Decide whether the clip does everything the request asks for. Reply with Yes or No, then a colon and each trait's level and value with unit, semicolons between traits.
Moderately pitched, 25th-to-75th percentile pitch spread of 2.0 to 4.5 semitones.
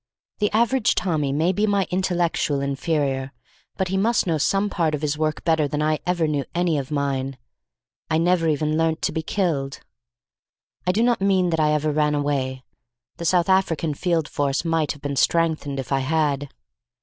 Yes: medium, 155 Hz; average, 3.7 semitones